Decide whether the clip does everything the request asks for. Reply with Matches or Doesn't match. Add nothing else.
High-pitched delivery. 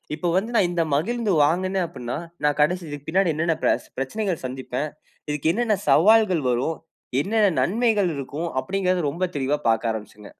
Doesn't match